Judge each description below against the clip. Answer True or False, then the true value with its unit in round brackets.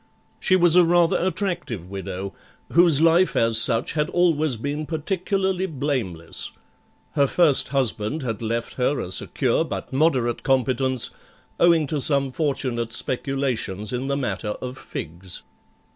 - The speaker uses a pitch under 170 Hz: True (135 Hz)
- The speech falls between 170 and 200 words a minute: False (135 wpm)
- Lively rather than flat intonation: True (6.0 semitones)